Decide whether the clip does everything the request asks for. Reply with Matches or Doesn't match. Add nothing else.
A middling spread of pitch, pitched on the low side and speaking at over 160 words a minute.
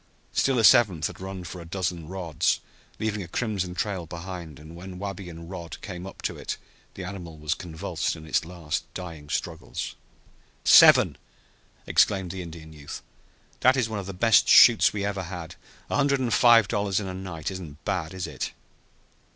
Matches